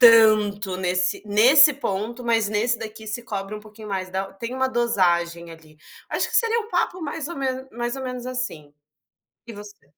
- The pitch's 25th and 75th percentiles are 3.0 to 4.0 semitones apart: No, average, 4.4 semitones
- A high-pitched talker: Yes, high, 215 Hz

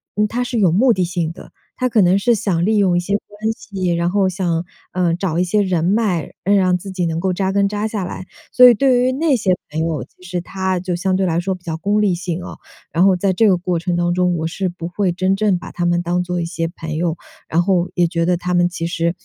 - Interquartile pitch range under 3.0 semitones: Yes, narrow, 2.5 semitones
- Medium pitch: Yes, medium, 180 Hz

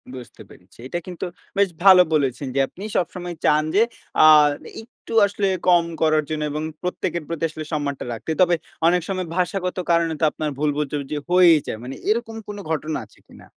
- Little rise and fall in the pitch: No, average, 3.2 semitones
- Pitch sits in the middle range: Yes, medium, 170 Hz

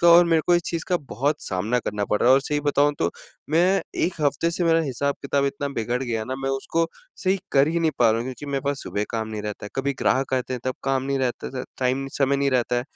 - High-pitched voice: No, low, 135 Hz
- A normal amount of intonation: Yes, average, 3.6 semitones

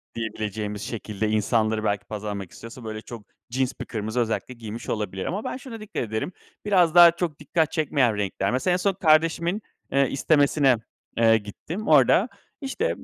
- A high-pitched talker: No, low, 120 Hz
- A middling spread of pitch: No, wide, 7.2 semitones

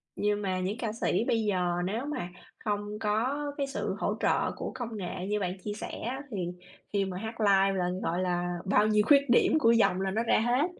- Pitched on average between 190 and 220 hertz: Yes, high, 210 Hz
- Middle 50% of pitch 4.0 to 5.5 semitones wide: No, average, 3.4 semitones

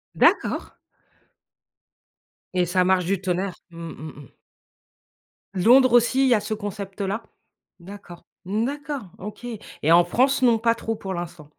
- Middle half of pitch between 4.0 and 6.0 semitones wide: Yes, average, 4.5 semitones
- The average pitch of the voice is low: No, high, 200 Hz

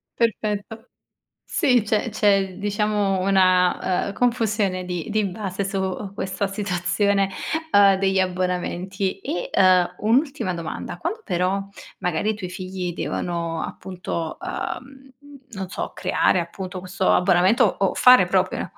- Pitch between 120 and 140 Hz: No, high, 190 Hz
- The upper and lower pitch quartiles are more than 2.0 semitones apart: Yes, narrow, 2.4 semitones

